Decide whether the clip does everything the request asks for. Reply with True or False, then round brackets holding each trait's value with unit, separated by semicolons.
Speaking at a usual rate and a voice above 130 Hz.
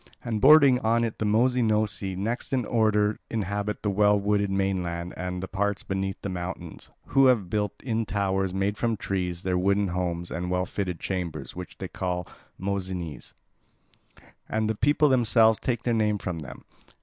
False (170 wpm; 100 Hz)